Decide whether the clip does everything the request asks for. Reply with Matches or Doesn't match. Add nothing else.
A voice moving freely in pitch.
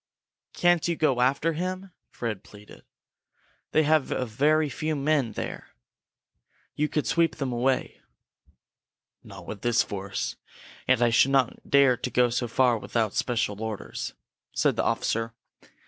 Doesn't match